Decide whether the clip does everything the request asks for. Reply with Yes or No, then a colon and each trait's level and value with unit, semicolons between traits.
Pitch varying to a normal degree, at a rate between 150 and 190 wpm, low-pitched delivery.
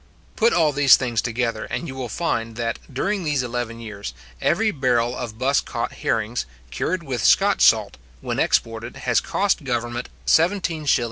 Yes: average, 4.6 semitones; average, 160 wpm; low, 125 Hz